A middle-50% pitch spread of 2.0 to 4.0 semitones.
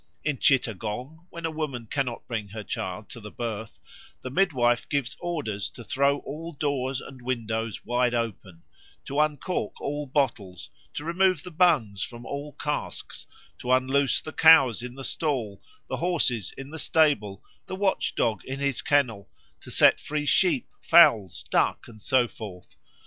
No: average, 5.0 semitones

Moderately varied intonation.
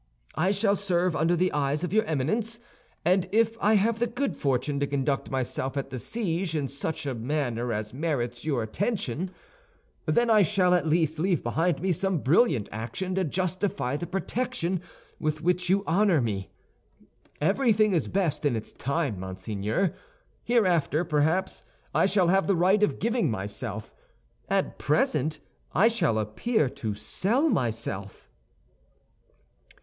No: wide, 6.6 semitones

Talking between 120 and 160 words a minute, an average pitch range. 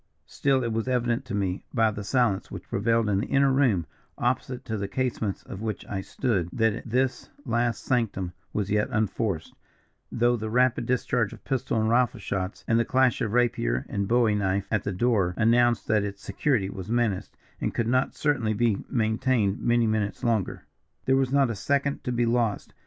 No: average, 190 wpm; average, 3.2 semitones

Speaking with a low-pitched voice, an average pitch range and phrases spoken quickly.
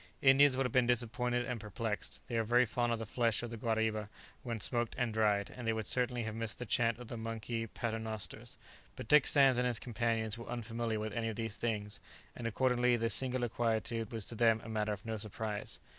No: low, 115 Hz; narrow, 1.7 semitones; fast, 220 wpm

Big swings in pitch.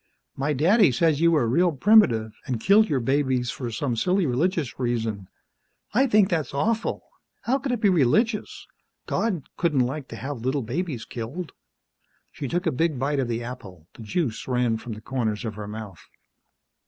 Yes: wide, 6.9 semitones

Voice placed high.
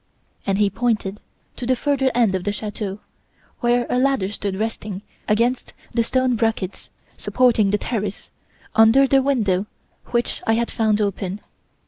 Yes: high, 225 Hz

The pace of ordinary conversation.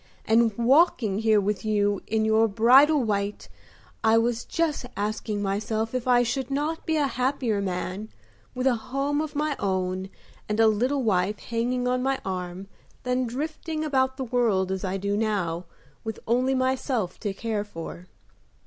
Yes: average, 165 wpm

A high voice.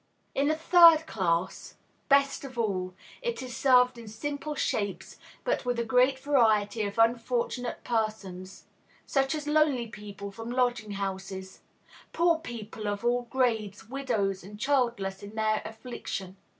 Yes: high, 235 Hz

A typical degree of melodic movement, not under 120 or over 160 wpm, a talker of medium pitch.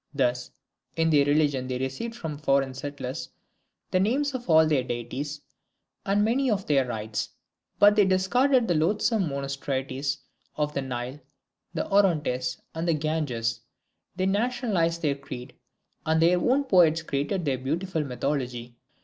No: wide, 6.1 semitones; average, 145 wpm; medium, 150 Hz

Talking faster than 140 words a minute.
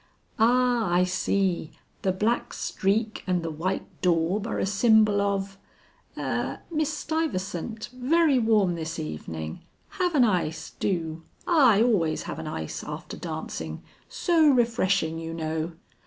No: slow, 135 wpm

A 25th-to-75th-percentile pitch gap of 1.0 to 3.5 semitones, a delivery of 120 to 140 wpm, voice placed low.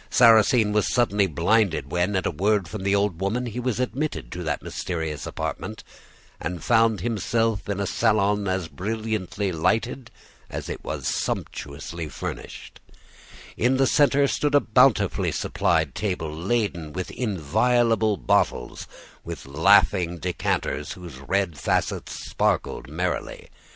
No: average, 5.1 semitones; slow, 135 wpm; low, 100 Hz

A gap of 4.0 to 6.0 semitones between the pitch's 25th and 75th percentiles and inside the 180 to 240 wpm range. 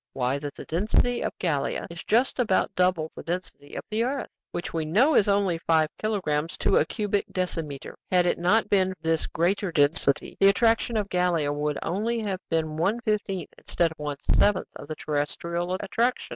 Yes: average, 4.6 semitones; average, 190 wpm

